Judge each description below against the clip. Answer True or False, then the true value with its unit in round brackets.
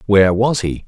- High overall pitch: False (105 Hz)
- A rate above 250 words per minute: False (205 wpm)